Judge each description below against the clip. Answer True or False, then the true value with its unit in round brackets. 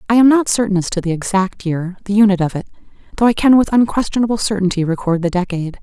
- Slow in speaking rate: False (205 wpm)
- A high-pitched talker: True (200 Hz)